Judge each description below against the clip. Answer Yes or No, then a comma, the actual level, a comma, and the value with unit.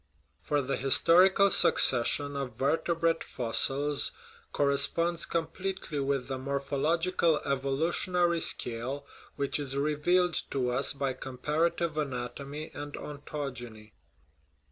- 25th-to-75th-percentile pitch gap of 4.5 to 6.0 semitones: No, average, 3.5 semitones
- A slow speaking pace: Yes, slow, 105 wpm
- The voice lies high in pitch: No, medium, 145 Hz